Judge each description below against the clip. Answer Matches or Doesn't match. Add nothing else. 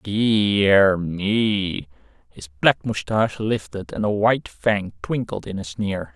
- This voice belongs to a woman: Doesn't match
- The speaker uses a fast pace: Doesn't match